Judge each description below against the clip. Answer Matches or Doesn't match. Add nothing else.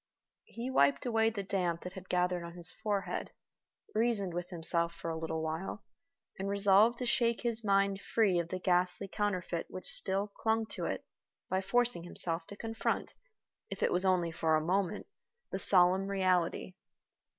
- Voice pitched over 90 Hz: Matches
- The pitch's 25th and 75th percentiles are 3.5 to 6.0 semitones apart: Doesn't match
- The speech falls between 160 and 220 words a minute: Matches